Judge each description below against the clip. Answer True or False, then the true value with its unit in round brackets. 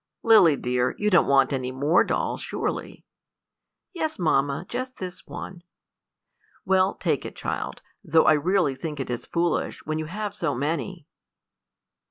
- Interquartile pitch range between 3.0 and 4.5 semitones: False (5.3 semitones)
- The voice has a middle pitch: True (165 Hz)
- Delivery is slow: False (150 wpm)